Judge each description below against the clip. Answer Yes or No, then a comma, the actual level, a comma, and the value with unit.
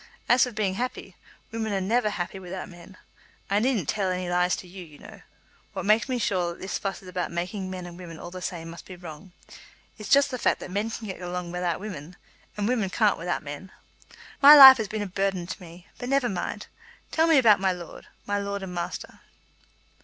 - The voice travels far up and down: No, average, 3.2 semitones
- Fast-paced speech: Yes, fast, 220 wpm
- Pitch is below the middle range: No, high, 190 Hz